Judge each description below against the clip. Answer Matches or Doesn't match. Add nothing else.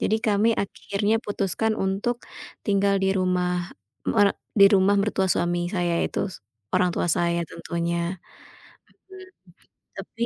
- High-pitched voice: Matches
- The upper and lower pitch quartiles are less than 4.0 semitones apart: Matches